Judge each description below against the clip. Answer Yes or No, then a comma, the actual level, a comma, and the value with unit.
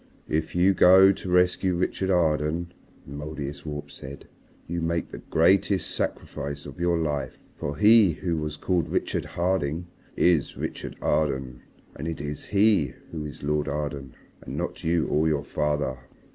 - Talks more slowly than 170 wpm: Yes, average, 155 wpm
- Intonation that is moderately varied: Yes, average, 3.4 semitones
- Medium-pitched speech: No, very low, 80 Hz